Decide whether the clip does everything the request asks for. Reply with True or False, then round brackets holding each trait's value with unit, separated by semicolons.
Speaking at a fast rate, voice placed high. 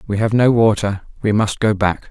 False (230 wpm; 105 Hz)